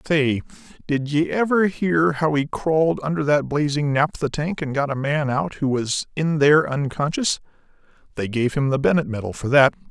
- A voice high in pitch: No, medium, 145 Hz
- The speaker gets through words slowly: No, average, 190 wpm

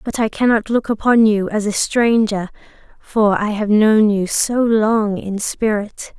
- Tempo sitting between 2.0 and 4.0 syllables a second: Yes, 3.9 syllables/s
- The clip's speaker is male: No, female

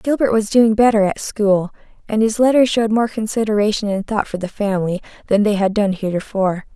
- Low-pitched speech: No, high, 210 Hz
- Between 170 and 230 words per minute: Yes, average, 195 wpm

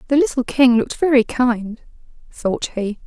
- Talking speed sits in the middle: Yes, average, 155 wpm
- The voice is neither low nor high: No, very high, 250 Hz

